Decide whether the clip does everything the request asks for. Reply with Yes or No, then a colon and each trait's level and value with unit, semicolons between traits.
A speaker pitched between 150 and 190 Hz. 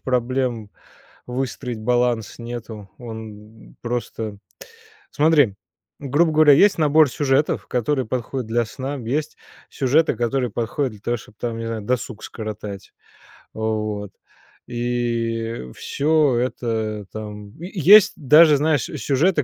No: low, 120 Hz